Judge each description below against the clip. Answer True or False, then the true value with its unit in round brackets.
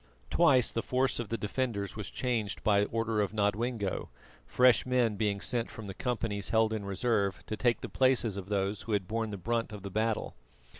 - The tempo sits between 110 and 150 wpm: False (200 wpm)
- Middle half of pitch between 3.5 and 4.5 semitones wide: False (2.7 semitones)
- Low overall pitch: True (110 Hz)